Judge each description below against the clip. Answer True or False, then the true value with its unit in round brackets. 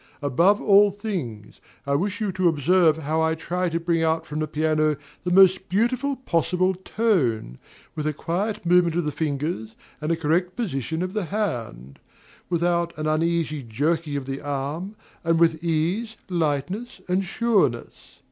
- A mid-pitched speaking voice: True (165 Hz)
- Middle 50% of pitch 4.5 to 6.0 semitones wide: False (3.7 semitones)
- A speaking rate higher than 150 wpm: True (160 wpm)